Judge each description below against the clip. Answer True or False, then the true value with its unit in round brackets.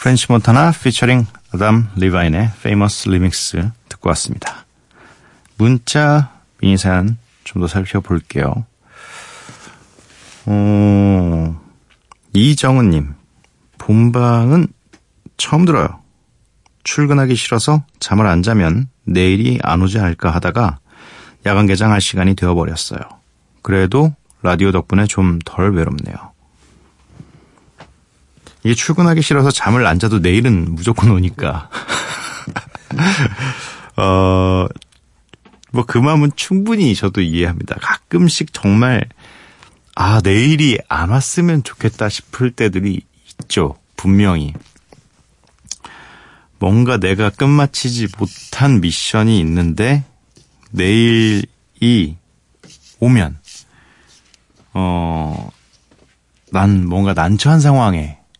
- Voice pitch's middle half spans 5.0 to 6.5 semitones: True (5.5 semitones)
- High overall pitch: False (105 Hz)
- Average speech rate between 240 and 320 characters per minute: False (205 characters per minute)